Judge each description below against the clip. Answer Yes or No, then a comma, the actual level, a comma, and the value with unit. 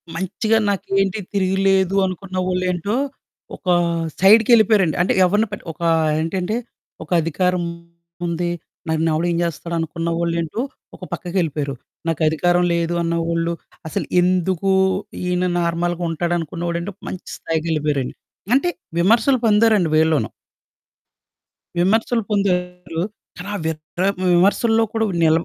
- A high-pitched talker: No, medium, 175 Hz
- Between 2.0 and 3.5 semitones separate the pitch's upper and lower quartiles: Yes, average, 2.7 semitones